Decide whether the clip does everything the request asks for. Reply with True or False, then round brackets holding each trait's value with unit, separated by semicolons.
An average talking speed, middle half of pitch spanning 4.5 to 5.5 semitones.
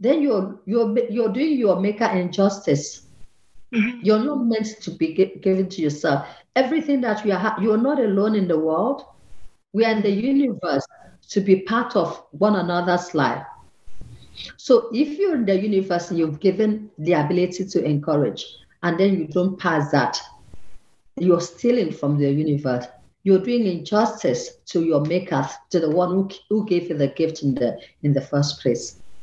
True (170 wpm; 5.0 semitones)